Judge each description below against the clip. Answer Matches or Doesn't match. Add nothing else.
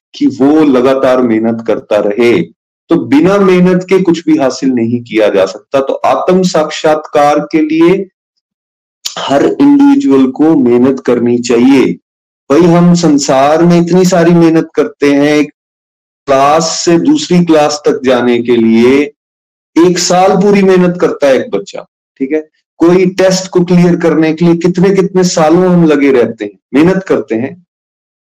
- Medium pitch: Matches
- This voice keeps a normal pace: Matches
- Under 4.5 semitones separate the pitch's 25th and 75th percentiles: Doesn't match